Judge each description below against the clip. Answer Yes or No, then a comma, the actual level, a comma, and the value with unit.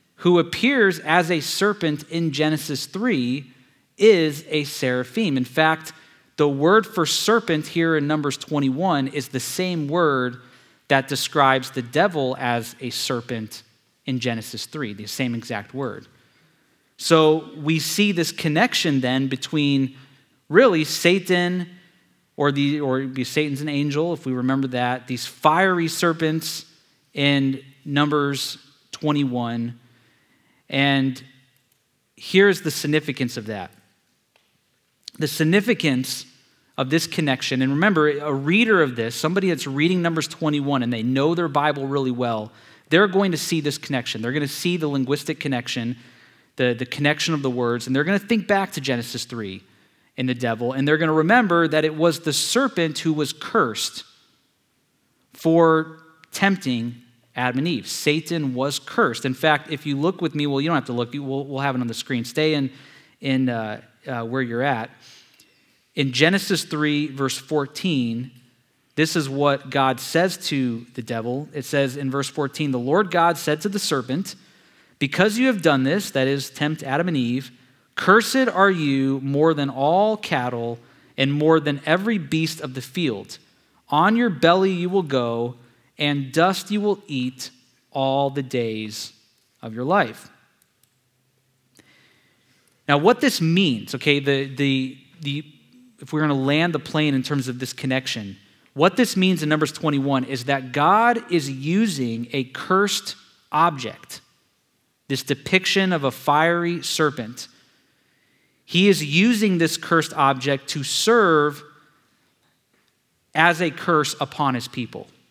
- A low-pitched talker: No, medium, 145 Hz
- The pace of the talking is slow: No, average, 155 wpm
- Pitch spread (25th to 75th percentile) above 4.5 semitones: No, average, 3.9 semitones